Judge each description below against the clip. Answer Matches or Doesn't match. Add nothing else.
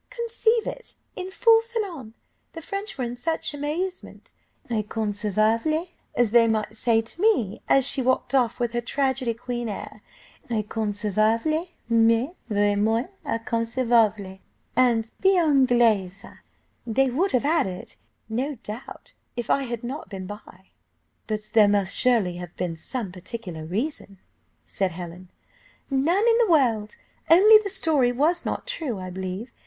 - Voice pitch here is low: Doesn't match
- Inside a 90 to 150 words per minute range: Matches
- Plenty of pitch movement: Matches